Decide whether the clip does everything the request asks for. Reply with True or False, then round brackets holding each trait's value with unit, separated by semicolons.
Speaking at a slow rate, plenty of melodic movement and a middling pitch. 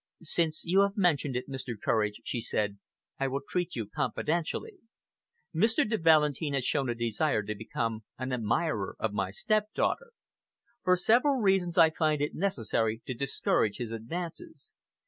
False (155 wpm; 7.6 semitones; 150 Hz)